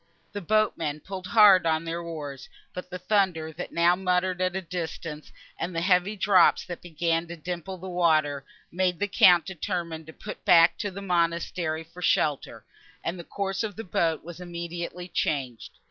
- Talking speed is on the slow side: No, average, 175 wpm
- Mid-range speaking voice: Yes, medium, 175 Hz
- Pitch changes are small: Yes, narrow, 2.1 semitones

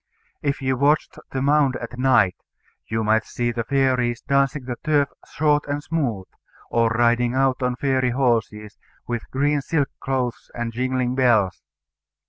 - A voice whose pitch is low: Yes, low, 130 Hz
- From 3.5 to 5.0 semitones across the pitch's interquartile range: No, average, 2.7 semitones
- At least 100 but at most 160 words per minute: Yes, average, 150 wpm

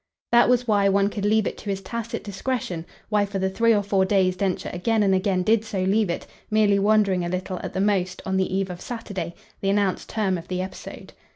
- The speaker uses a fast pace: Yes, fast, 235 wpm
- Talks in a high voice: Yes, high, 195 Hz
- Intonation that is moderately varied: No, narrow, 2.2 semitones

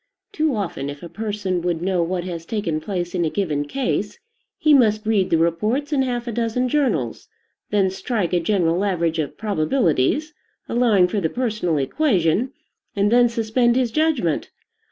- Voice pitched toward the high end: Yes, high, 205 Hz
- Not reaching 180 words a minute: Yes, average, 170 wpm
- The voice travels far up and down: Yes, wide, 6.0 semitones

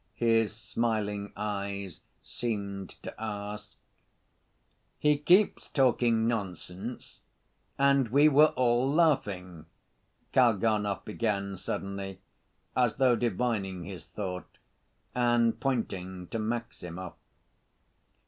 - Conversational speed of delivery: No, slow, 90 wpm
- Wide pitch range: No, average, 3.5 semitones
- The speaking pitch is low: Yes, low, 110 Hz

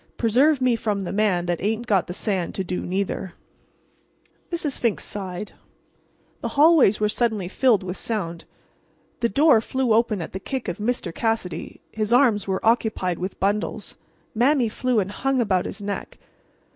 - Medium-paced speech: Yes, average, 165 wpm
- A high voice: Yes, high, 215 Hz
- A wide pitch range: No, average, 4.1 semitones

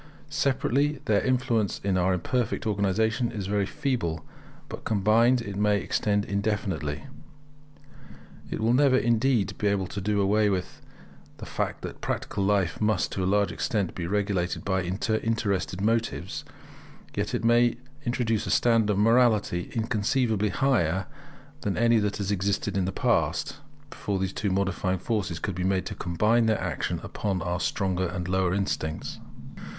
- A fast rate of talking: No, average, 155 wpm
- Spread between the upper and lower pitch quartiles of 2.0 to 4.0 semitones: Yes, average, 3.3 semitones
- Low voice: Yes, low, 100 Hz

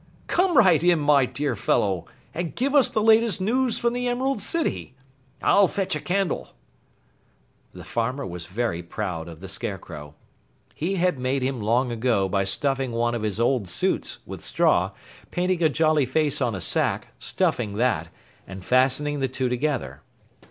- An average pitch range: No, wide, 8.6 semitones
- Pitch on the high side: No, low, 130 Hz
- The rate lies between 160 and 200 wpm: Yes, average, 165 wpm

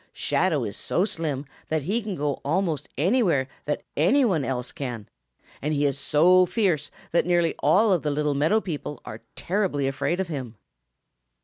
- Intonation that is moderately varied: Yes, average, 4.6 semitones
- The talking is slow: No, average, 175 wpm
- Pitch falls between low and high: Yes, medium, 155 Hz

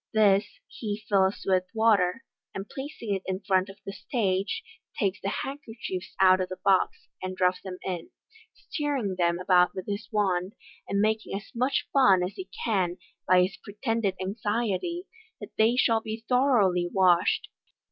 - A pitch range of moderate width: Yes, average, 3.3 semitones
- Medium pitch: No, high, 195 Hz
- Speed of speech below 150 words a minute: No, average, 165 wpm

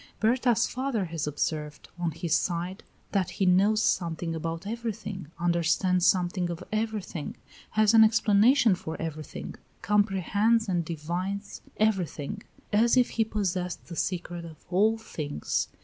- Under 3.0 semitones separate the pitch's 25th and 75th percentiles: No, average, 4.3 semitones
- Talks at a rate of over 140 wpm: No, slow, 135 wpm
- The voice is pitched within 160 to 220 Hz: Yes, medium, 185 Hz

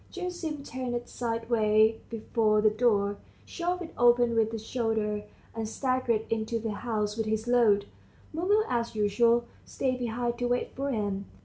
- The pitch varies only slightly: Yes, narrow, 2.3 semitones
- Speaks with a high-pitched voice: Yes, high, 230 Hz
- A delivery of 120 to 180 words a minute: Yes, average, 150 wpm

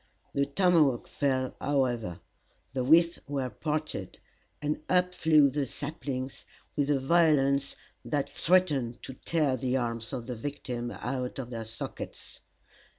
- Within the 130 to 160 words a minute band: Yes, slow, 135 wpm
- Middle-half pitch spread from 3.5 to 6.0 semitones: No, average, 3.1 semitones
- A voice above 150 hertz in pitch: No, medium, 140 Hz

